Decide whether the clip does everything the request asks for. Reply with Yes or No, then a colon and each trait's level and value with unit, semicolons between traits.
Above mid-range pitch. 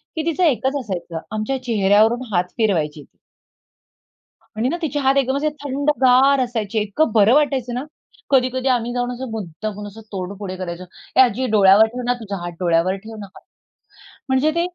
Yes: high, 235 Hz